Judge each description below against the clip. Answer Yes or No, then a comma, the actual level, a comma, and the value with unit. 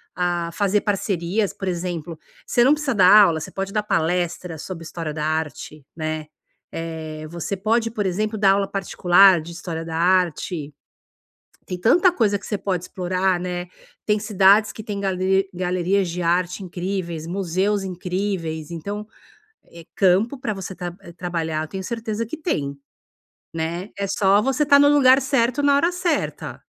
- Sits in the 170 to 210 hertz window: Yes, medium, 185 Hz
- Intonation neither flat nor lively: Yes, average, 3.5 semitones